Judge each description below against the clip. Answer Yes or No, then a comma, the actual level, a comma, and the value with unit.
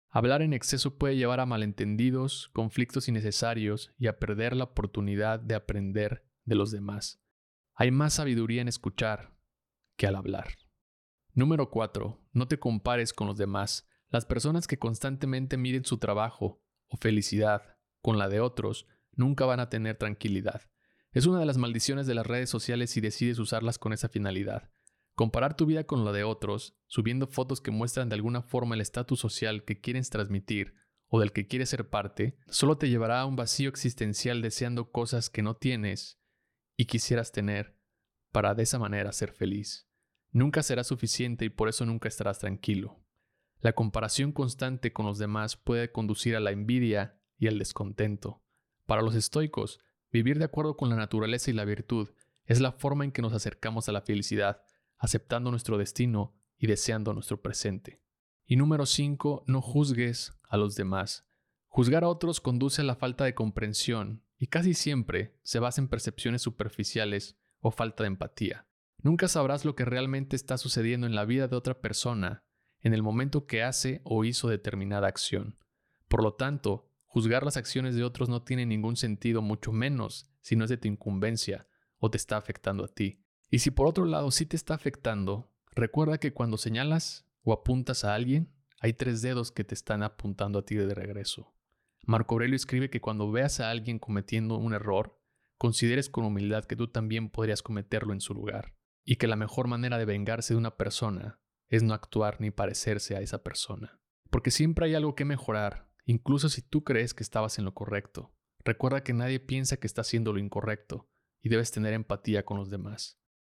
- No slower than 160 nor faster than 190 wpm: Yes, average, 180 wpm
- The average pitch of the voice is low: Yes, low, 115 Hz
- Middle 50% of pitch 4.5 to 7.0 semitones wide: No, average, 3.3 semitones